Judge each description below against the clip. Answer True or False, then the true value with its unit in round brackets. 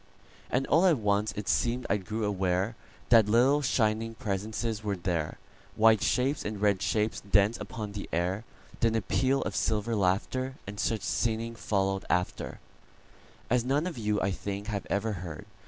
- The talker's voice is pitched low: True (105 Hz)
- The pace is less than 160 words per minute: True (150 wpm)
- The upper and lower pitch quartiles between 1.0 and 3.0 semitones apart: True (2.6 semitones)